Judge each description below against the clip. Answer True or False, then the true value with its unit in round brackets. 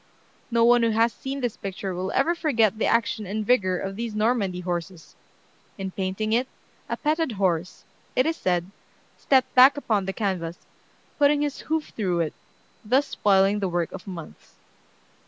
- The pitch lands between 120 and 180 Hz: False (210 Hz)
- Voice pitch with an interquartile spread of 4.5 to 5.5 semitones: True (5.0 semitones)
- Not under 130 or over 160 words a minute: False (170 wpm)